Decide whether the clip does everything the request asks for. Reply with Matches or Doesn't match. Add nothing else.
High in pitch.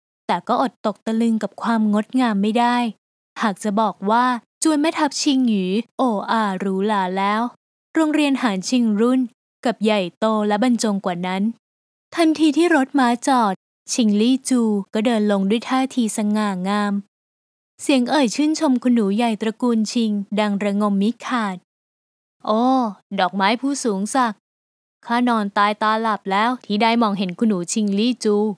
Matches